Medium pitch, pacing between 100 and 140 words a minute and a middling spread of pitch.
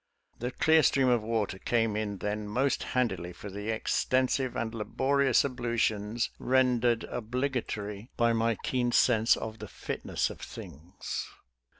No: low, 115 Hz; slow, 135 wpm; average, 3.1 semitones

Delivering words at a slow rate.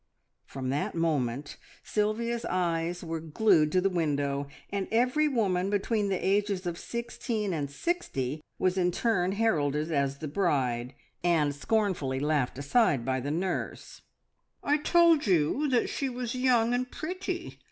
No: average, 145 wpm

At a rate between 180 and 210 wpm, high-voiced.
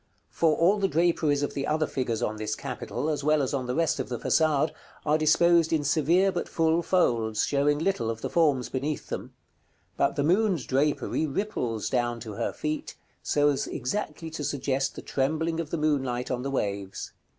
No: average, 195 wpm; medium, 145 Hz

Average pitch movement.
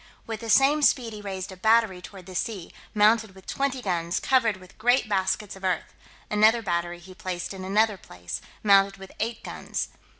Yes: average, 3.2 semitones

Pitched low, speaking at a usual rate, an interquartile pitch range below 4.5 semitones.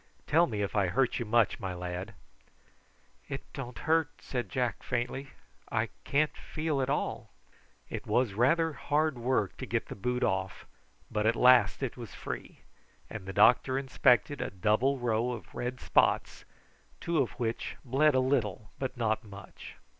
Yes: low, 125 Hz; average, 165 wpm; average, 4.1 semitones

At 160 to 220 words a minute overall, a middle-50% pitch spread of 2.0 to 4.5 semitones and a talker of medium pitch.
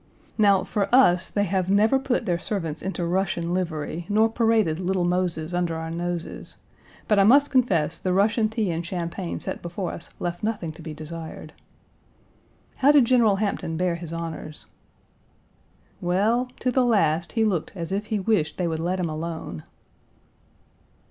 Yes: average, 165 wpm; average, 4.2 semitones; medium, 180 Hz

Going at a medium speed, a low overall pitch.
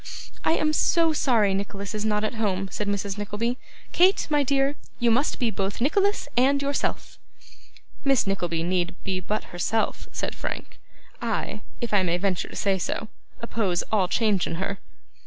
No: average, 170 wpm; high, 210 Hz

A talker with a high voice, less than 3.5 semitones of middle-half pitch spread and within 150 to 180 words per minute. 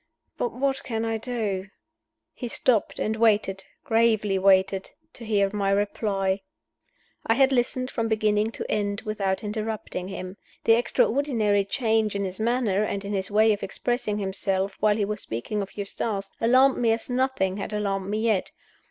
Yes: high, 210 Hz; narrow, 2.5 semitones; average, 165 wpm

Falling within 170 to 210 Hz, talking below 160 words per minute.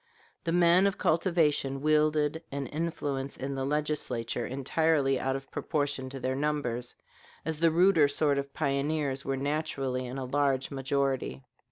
No: medium, 140 Hz; average, 150 wpm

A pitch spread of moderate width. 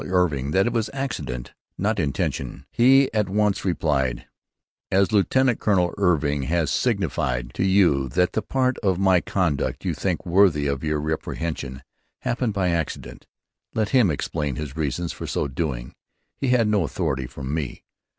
No: wide, 6.2 semitones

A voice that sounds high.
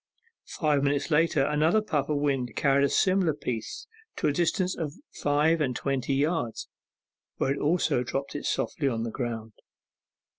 No: medium, 145 Hz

